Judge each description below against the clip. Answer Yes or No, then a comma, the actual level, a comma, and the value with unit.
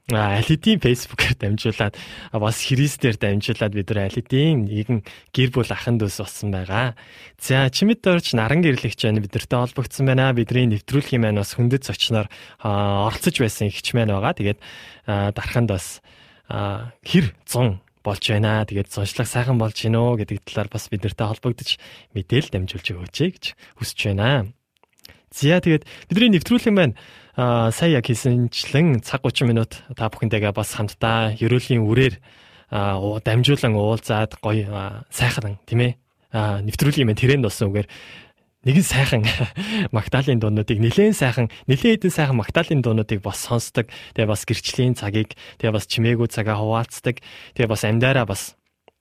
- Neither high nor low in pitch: No, low, 115 Hz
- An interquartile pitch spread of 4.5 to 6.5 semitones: No, average, 3.5 semitones